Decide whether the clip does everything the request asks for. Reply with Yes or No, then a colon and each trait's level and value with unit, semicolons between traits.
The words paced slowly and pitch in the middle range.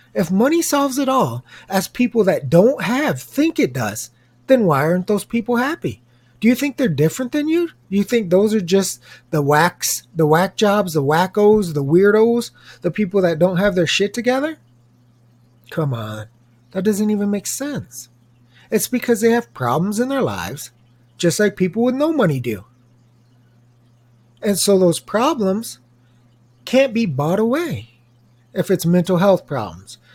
No: average, 165 wpm; medium, 180 Hz